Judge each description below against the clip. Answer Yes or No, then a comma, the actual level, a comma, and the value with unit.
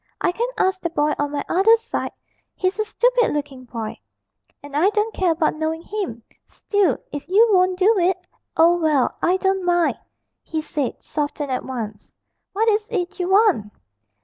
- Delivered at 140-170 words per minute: No, average, 180 wpm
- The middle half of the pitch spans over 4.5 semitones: Yes, average, 5.3 semitones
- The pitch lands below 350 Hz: No, very high, 355 Hz